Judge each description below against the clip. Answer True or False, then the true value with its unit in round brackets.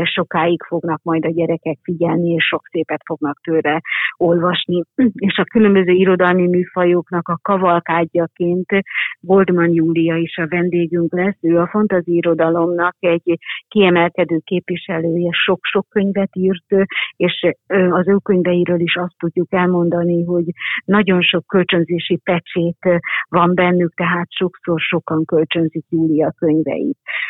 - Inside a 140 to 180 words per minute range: False (125 wpm)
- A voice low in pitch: False (175 Hz)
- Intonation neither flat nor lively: False (1.4 semitones)